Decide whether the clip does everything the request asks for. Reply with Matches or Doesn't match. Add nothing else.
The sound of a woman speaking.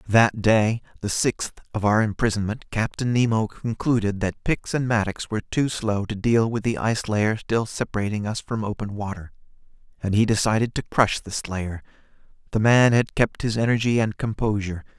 Doesn't match